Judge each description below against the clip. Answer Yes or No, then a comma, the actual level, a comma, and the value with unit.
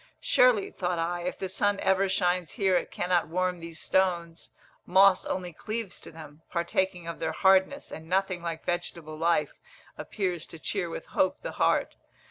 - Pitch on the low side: No, medium, 180 Hz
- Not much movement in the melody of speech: Yes, narrow, 2.2 semitones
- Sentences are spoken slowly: No, average, 170 wpm